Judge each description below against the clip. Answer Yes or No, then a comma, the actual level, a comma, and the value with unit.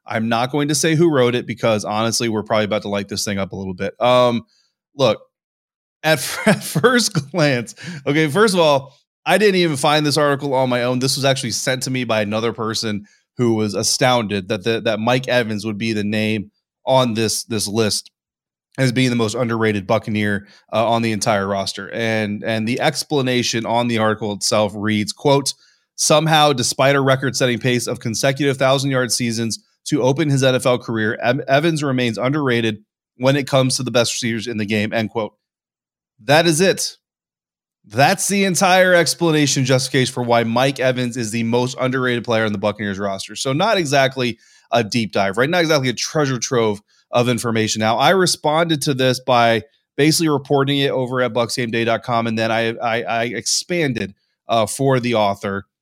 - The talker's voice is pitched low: Yes, low, 125 Hz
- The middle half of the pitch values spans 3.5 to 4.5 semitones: Yes, average, 3.9 semitones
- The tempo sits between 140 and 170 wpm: No, average, 190 wpm